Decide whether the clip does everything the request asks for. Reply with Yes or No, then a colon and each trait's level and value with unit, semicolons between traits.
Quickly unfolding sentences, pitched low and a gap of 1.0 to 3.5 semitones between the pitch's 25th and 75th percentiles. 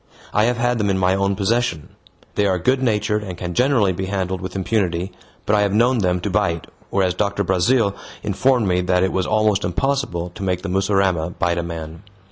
Yes: fast, 210 wpm; very low, 95 Hz; average, 2.9 semitones